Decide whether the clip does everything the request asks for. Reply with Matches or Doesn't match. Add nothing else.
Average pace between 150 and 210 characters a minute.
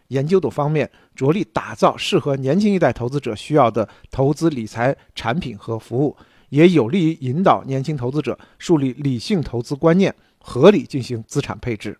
Doesn't match